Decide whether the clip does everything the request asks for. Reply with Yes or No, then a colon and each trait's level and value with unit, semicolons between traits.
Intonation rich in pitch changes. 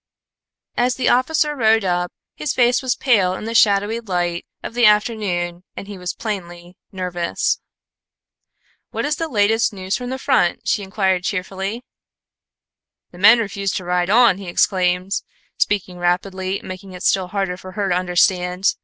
No: average, 3.7 semitones